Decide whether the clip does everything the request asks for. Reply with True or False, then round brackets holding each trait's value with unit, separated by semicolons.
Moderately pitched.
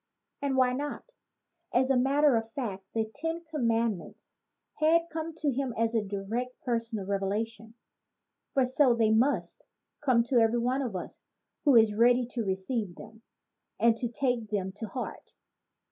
False (235 Hz)